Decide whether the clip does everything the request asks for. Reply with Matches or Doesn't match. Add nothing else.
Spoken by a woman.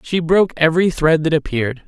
Doesn't match